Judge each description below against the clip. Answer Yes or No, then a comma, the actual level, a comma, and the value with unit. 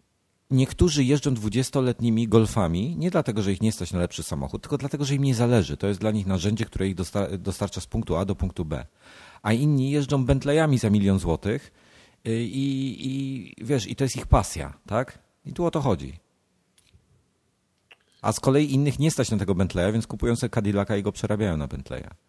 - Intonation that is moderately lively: No, wide, 5.8 semitones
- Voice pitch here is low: Yes, low, 110 Hz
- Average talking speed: No, fast, 195 wpm